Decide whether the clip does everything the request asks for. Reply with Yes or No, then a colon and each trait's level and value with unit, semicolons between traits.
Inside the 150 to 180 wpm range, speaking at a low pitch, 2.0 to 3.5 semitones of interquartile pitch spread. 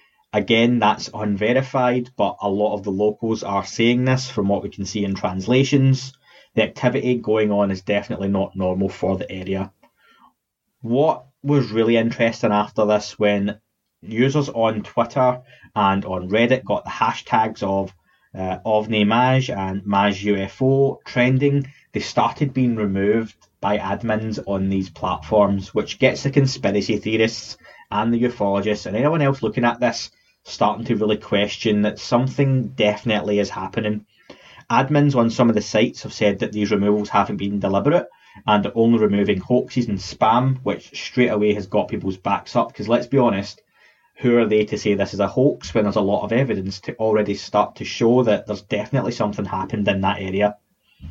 Yes: average, 175 wpm; low, 105 Hz; average, 3.2 semitones